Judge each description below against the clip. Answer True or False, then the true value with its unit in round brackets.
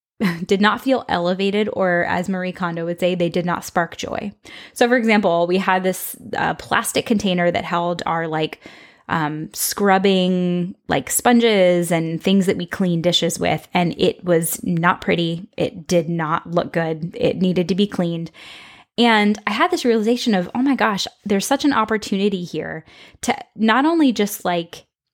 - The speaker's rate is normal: True (175 wpm)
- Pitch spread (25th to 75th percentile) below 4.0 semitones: True (3.6 semitones)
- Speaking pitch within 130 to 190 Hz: True (185 Hz)